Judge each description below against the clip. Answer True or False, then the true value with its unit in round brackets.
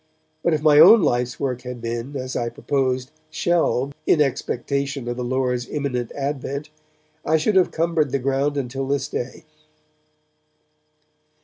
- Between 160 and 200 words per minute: False (145 wpm)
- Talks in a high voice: False (135 Hz)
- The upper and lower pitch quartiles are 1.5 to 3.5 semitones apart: True (2.9 semitones)